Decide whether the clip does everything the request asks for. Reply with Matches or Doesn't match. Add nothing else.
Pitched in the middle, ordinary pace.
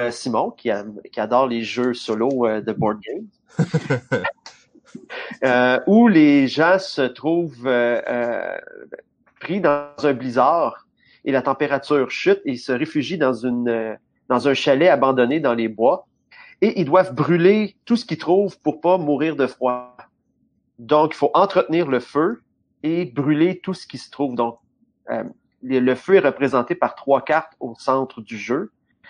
Matches